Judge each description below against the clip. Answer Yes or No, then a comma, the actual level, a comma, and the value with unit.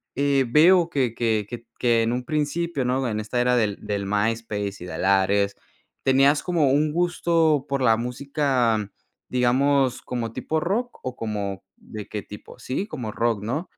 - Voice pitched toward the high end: No, low, 125 Hz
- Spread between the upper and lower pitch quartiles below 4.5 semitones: No, average, 4.8 semitones